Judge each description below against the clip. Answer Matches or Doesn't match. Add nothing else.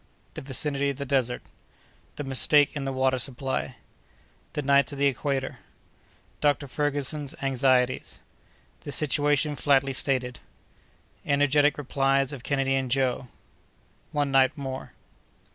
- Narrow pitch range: Matches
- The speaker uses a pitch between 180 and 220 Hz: Doesn't match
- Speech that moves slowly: Matches